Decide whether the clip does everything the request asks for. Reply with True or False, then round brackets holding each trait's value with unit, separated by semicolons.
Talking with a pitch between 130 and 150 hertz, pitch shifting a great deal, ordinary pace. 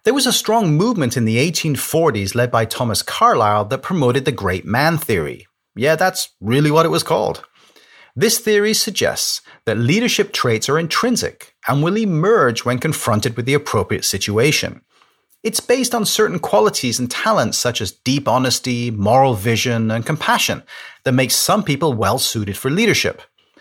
True (135 Hz; 7.2 semitones; 165 wpm)